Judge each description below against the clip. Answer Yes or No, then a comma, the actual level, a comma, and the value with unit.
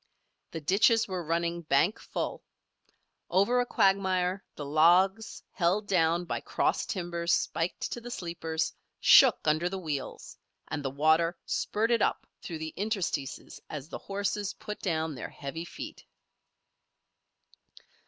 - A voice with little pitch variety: No, average, 3.6 semitones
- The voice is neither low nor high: Yes, medium, 175 Hz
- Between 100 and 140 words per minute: Yes, slow, 135 wpm